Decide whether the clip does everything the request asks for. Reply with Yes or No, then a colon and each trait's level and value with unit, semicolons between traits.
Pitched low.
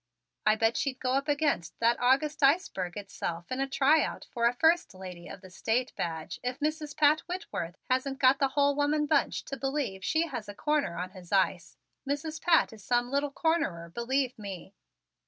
No: very high, 260 Hz